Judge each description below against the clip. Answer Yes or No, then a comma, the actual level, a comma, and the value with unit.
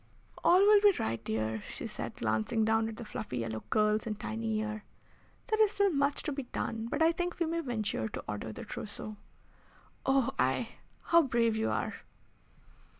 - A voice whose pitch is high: Yes, high, 225 Hz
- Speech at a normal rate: Yes, average, 185 wpm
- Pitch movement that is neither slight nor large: No, wide, 6.9 semitones